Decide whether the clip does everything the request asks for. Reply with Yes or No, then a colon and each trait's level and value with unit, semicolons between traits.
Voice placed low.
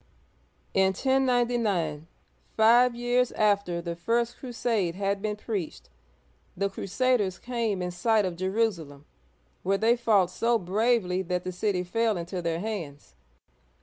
No: high, 200 Hz